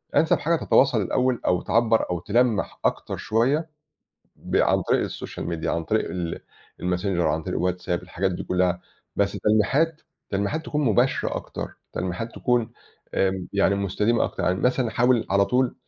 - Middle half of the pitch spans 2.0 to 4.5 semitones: No, average, 5.2 semitones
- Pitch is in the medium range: No, low, 100 Hz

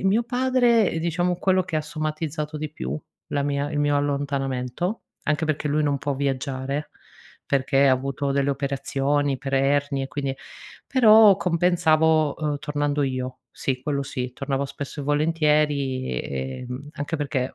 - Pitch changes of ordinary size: No, narrow, 2.3 semitones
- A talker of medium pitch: Yes, medium, 145 Hz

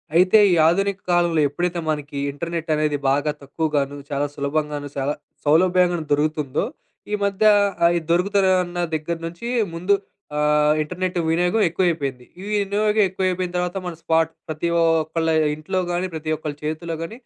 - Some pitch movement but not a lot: Yes, average, 3.0 semitones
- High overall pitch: No, medium, 165 Hz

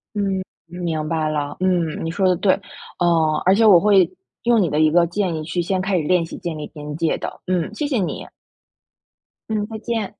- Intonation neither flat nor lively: Yes, average, 3.7 semitones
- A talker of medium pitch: Yes, medium, 175 Hz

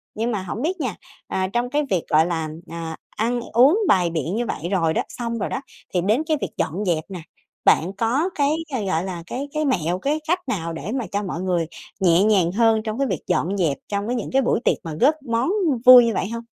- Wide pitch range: Yes, wide, 6.0 semitones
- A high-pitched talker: Yes, high, 210 Hz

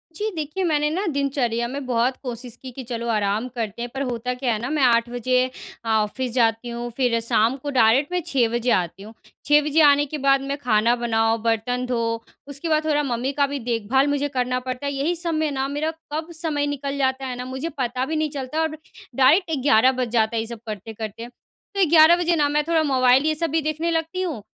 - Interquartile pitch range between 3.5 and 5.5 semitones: Yes, average, 4.1 semitones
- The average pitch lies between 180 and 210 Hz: No, very high, 260 Hz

